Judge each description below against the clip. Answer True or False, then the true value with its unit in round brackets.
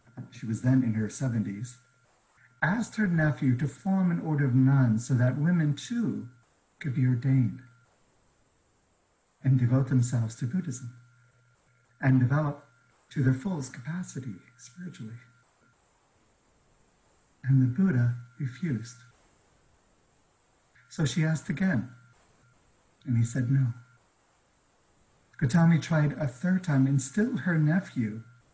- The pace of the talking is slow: True (115 wpm)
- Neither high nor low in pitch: False (130 Hz)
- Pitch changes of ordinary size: True (3.7 semitones)